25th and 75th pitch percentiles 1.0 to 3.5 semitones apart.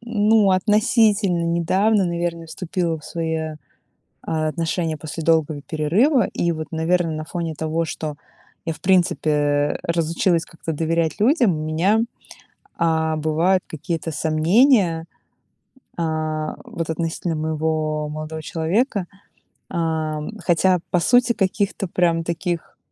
Yes: average, 2.8 semitones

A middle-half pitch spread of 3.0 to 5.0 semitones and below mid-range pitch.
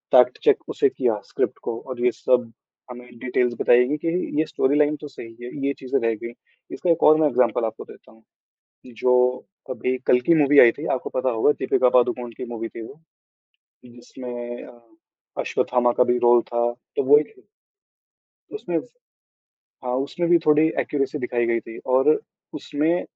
Yes: average, 3.4 semitones; low, 125 Hz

